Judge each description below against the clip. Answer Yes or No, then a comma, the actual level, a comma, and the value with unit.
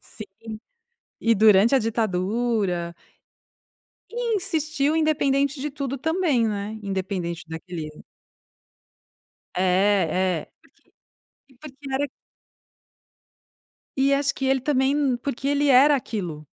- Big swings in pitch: Yes, wide, 6.7 semitones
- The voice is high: Yes, high, 245 Hz